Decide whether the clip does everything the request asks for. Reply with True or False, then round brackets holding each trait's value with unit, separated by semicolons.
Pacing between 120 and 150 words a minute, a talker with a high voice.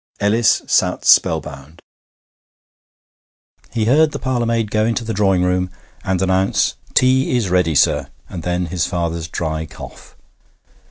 False (140 wpm; 95 Hz)